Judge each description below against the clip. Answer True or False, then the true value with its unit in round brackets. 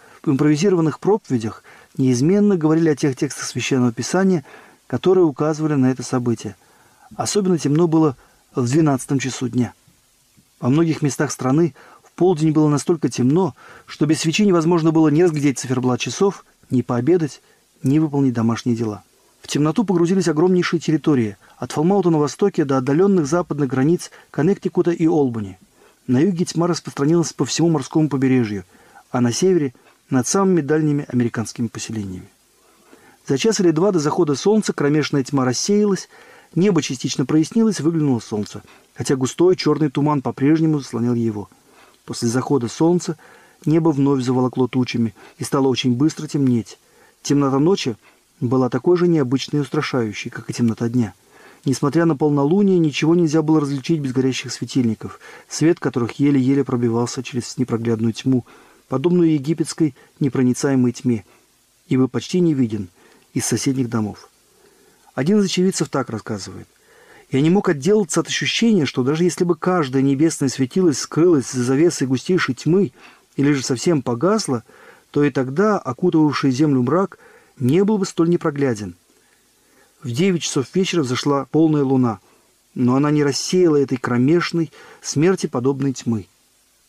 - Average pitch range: True (4.9 semitones)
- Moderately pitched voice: True (145 Hz)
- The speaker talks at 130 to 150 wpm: True (145 wpm)